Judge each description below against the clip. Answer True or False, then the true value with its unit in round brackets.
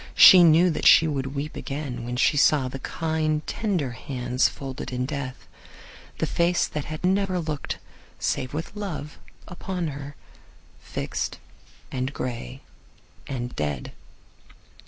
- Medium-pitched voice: True (145 Hz)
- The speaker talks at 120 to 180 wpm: True (135 wpm)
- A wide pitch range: False (4.2 semitones)